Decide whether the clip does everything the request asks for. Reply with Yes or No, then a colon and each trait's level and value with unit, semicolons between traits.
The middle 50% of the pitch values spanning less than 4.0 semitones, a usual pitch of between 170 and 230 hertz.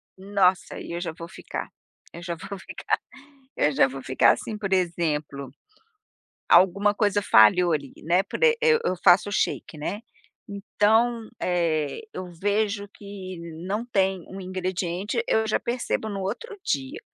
Yes: average, 3.3 semitones; high, 190 Hz